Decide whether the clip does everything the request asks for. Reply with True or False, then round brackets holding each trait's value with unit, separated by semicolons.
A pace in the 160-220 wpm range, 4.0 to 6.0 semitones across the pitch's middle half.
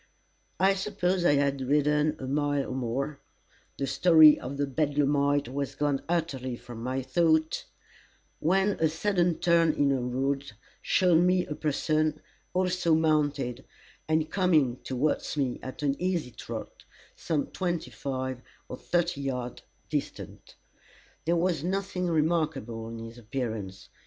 False (135 wpm; 4.3 semitones)